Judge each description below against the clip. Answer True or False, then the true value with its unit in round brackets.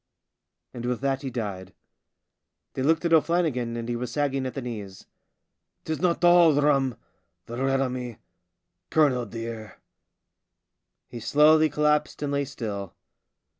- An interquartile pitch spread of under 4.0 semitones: False (4.3 semitones)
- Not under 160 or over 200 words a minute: False (145 wpm)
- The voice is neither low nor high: False (130 Hz)